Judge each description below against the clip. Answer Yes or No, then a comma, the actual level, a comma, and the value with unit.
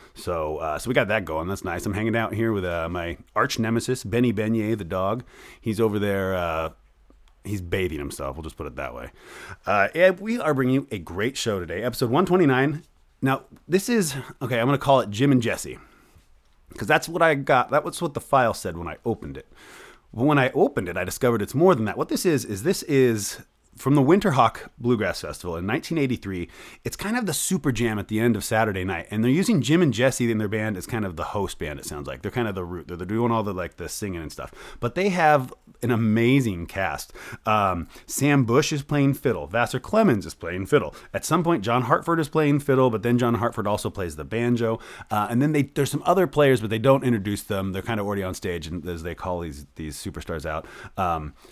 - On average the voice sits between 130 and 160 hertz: No, low, 115 Hz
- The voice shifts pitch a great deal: Yes, wide, 5.9 semitones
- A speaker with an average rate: No, fast, 235 wpm